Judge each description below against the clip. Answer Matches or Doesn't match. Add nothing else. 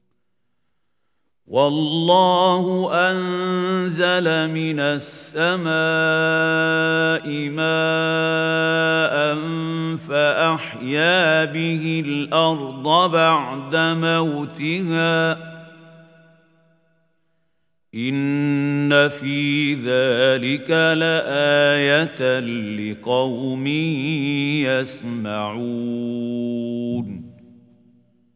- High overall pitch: Doesn't match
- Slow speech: Matches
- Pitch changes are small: Doesn't match